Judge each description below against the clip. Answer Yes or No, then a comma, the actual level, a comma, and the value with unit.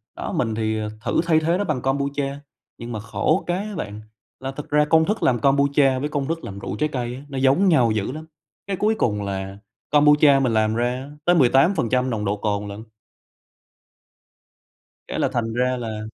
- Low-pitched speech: Yes, low, 130 Hz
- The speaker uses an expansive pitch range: No, average, 5.0 semitones